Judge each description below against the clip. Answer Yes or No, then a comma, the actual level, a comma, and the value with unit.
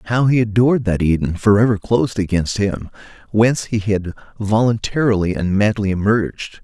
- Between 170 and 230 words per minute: No, average, 145 wpm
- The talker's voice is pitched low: Yes, low, 105 Hz